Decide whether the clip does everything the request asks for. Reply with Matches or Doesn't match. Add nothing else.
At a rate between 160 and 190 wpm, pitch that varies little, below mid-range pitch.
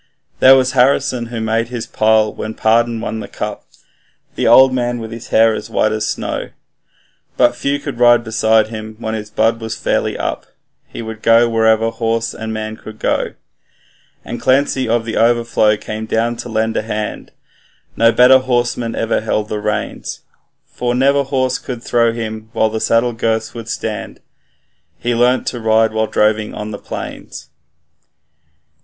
Matches